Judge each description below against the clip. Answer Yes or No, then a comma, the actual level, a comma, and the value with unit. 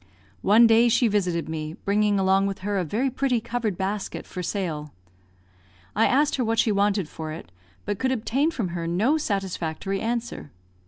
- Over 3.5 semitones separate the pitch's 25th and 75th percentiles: Yes, average, 4.3 semitones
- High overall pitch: Yes, high, 205 Hz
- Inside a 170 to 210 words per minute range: Yes, average, 175 wpm